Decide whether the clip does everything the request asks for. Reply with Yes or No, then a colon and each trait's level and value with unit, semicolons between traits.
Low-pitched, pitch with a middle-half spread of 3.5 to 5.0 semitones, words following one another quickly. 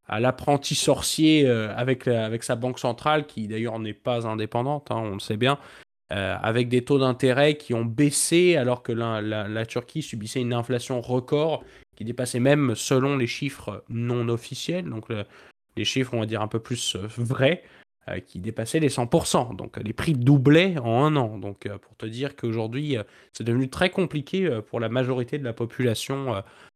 No: low, 125 Hz; average, 3.9 semitones; average, 185 wpm